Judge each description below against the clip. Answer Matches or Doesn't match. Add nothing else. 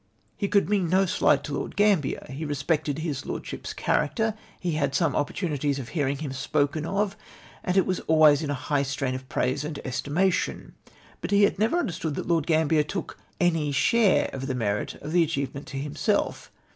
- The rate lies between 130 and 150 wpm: Doesn't match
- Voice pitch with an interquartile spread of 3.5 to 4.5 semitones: Matches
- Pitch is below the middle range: Doesn't match